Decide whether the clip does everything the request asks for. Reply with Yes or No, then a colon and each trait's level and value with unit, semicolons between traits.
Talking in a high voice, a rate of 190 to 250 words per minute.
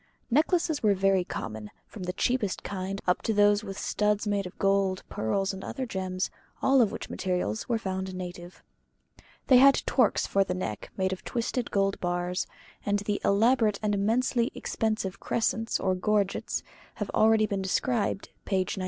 No: high, 200 Hz; average, 170 wpm